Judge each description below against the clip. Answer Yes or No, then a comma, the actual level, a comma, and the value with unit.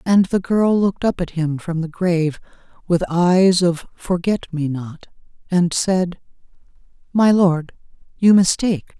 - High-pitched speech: No, medium, 175 Hz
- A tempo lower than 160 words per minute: Yes, average, 145 wpm